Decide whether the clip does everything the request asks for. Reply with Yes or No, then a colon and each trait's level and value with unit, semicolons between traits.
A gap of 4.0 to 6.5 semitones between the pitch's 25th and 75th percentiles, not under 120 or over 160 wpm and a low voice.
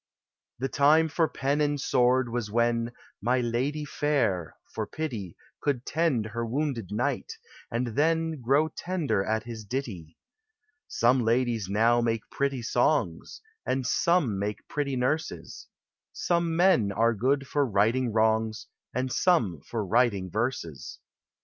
Yes: average, 4.6 semitones; average, 140 wpm; low, 120 Hz